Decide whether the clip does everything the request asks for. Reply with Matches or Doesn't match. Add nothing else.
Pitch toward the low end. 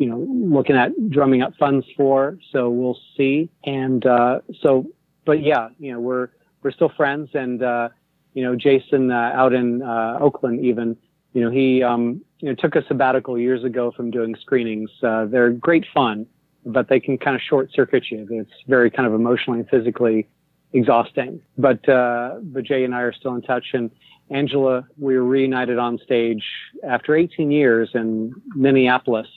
Matches